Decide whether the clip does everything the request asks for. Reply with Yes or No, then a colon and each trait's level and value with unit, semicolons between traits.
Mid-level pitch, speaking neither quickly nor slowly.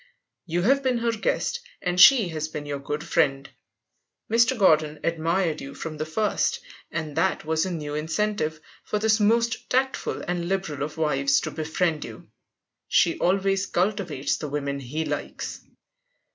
Yes: medium, 165 Hz; average, 160 wpm